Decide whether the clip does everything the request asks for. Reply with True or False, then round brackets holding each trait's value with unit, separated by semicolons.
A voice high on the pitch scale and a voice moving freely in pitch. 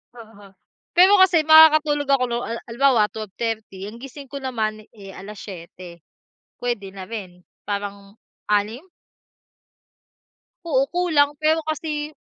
True (230 Hz; 6.4 semitones)